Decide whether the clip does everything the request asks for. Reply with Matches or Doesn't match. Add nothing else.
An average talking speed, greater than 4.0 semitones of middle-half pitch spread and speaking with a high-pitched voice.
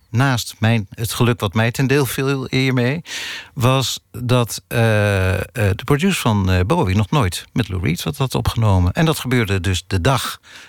Doesn't match